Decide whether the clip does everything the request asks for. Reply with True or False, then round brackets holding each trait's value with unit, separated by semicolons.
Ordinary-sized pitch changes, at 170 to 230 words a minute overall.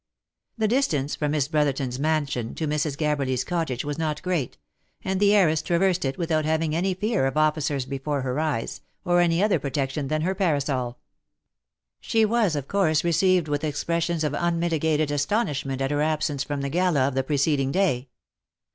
True (3.6 semitones; 180 wpm)